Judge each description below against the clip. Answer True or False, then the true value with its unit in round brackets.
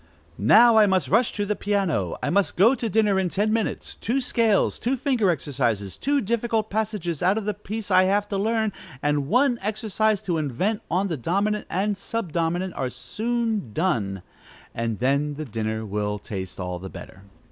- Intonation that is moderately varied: False (7.7 semitones)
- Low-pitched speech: False (195 Hz)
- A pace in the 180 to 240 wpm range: True (185 wpm)